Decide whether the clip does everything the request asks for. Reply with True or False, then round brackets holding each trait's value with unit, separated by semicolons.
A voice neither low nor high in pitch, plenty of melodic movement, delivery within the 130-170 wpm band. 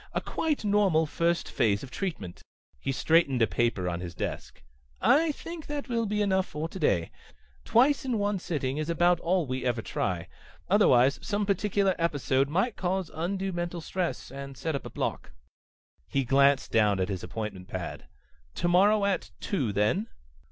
True (165 Hz; 7.9 semitones; 165 wpm)